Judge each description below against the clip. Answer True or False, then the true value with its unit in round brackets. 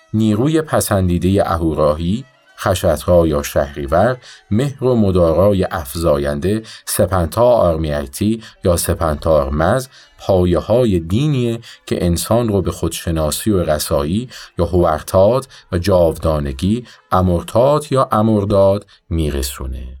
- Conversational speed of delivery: True (100 wpm)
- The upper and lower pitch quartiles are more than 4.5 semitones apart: True (5.0 semitones)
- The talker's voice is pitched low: True (90 Hz)